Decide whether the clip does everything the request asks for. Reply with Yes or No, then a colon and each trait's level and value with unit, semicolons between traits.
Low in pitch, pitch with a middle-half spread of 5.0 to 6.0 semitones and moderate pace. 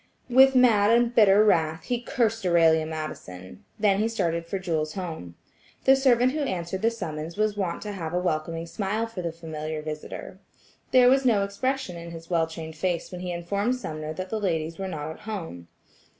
No: medium, 180 Hz; average, 5.3 semitones; average, 195 wpm